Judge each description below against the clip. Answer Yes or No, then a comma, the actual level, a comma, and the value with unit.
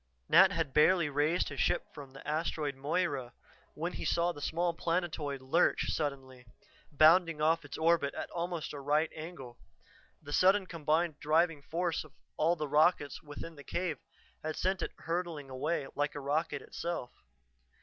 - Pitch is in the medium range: Yes, medium, 155 Hz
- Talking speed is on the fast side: No, average, 160 wpm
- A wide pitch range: No, average, 2.9 semitones